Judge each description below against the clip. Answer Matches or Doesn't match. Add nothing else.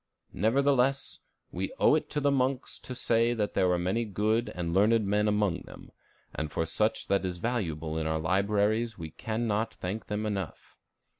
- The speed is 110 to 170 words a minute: Doesn't match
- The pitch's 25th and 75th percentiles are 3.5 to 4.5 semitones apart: Matches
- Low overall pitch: Matches